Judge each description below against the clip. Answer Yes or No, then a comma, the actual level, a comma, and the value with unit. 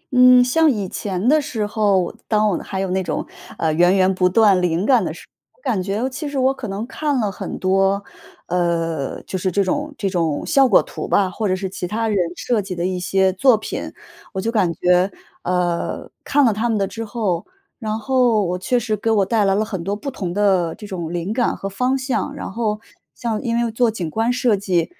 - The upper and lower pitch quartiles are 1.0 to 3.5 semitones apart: No, average, 4.1 semitones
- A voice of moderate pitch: No, high, 205 Hz